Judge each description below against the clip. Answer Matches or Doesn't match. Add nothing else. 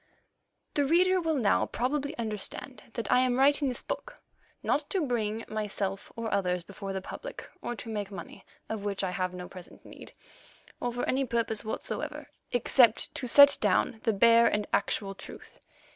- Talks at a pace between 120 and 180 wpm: Matches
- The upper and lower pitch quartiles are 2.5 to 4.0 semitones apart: Doesn't match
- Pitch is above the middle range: Matches